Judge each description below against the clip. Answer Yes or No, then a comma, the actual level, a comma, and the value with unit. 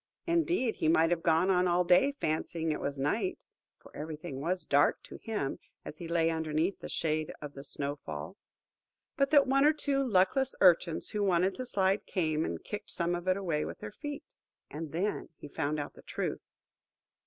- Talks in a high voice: No, medium, 175 Hz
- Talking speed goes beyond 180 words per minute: Yes, average, 200 wpm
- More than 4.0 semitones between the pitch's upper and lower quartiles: Yes, average, 5.1 semitones